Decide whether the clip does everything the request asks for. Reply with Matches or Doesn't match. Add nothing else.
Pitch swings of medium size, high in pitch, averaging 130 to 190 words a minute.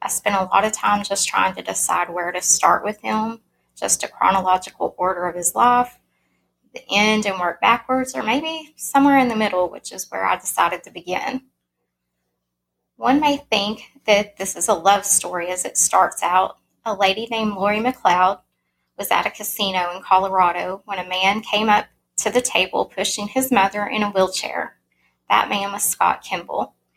Matches